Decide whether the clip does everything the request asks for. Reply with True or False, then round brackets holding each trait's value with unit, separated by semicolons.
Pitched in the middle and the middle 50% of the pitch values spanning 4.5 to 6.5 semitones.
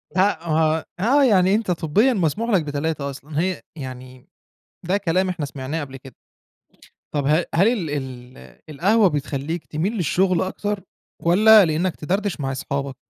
True (165 Hz; 5.5 semitones)